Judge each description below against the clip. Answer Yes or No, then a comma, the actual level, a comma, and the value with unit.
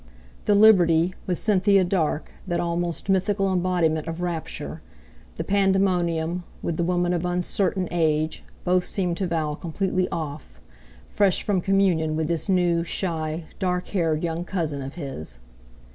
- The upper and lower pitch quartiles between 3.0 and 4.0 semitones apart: No, narrow, 2.5 semitones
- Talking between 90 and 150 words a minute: Yes, average, 140 wpm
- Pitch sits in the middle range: Yes, medium, 175 Hz